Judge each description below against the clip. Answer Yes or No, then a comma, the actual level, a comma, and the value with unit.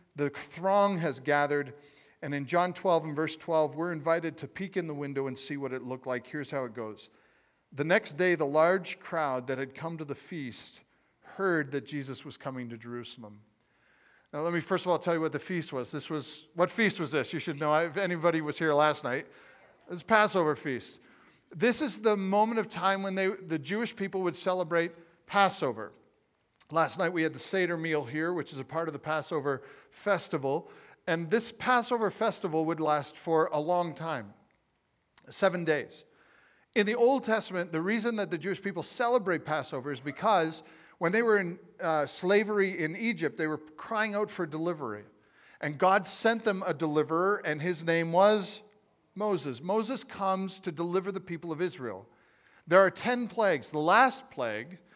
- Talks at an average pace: Yes, average, 190 wpm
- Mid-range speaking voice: Yes, medium, 170 Hz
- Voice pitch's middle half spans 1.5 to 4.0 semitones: No, average, 4.5 semitones